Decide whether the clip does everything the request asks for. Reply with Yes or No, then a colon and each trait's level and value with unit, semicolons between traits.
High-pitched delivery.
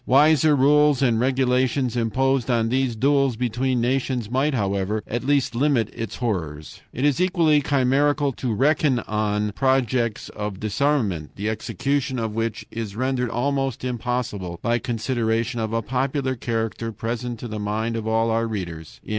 No: low, 120 Hz